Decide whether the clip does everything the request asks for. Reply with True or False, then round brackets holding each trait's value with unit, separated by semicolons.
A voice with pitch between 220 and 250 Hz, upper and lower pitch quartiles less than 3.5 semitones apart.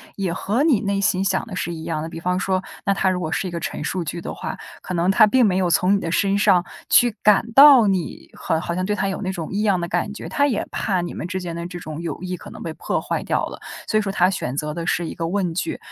False (185 Hz; 2.8 semitones)